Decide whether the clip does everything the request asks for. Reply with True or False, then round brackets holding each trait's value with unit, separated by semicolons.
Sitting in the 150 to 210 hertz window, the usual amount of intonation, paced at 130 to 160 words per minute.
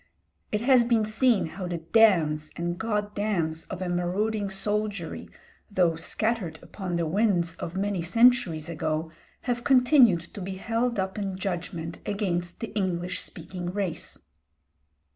True (190 Hz; 4.0 semitones; 140 wpm)